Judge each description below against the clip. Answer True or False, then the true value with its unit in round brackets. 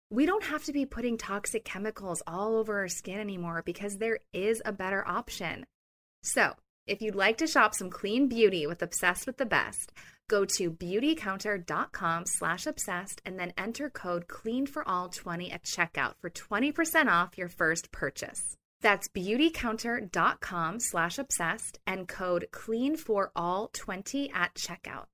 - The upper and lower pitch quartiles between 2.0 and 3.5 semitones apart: False (4.6 semitones)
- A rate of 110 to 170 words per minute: True (160 wpm)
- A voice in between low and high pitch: False (205 Hz)